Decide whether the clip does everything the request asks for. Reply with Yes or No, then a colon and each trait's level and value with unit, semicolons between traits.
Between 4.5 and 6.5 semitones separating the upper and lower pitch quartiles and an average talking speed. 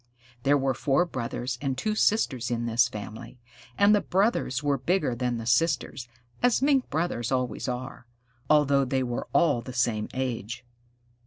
No: average, 4.0 semitones; average, 160 wpm